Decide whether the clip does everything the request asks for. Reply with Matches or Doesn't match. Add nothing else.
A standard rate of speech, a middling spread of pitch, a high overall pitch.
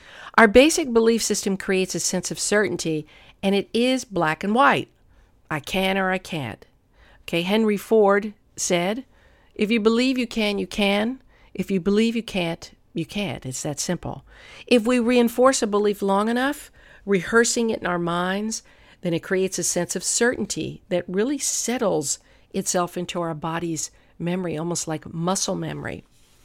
Matches